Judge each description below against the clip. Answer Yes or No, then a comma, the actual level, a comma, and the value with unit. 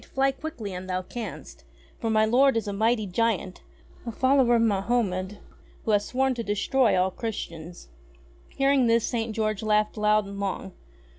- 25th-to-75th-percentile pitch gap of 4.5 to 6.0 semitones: No, average, 3.3 semitones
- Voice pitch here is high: Yes, high, 220 Hz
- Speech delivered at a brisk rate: No, average, 165 wpm